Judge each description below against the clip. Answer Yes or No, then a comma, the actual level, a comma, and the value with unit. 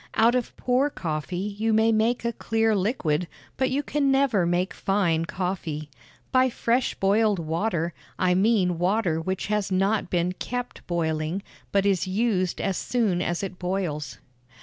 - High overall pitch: Yes, high, 195 Hz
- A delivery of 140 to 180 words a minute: Yes, average, 155 wpm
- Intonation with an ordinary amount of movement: Yes, average, 4.3 semitones